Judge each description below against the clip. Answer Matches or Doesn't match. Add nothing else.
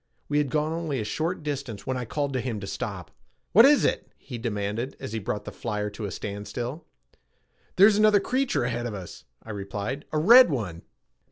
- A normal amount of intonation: Doesn't match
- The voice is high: Doesn't match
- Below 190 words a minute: Doesn't match